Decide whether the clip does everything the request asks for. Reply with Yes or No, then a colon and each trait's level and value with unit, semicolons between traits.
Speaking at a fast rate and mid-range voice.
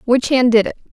No: fast, 250 wpm; high, 245 Hz